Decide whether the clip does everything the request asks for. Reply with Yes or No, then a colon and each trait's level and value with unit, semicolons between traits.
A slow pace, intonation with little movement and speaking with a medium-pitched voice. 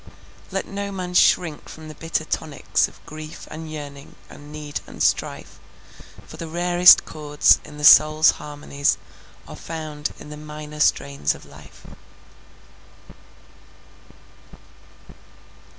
Yes: slow, 120 wpm; narrow, 1.4 semitones; medium, 155 Hz